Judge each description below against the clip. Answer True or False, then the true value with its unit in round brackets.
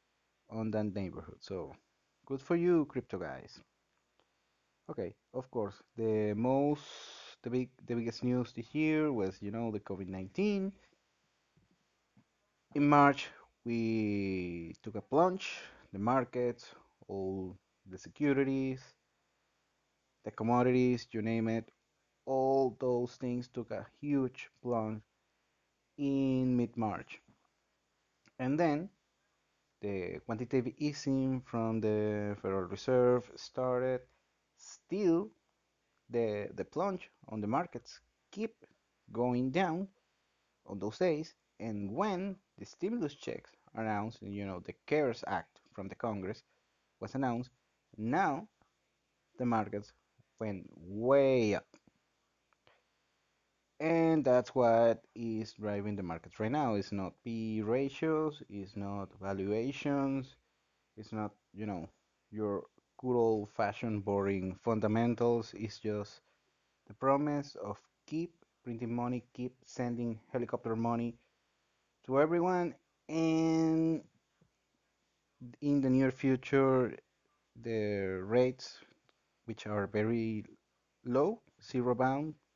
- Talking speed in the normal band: False (110 wpm)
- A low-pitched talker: True (120 Hz)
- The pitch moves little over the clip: False (4.3 semitones)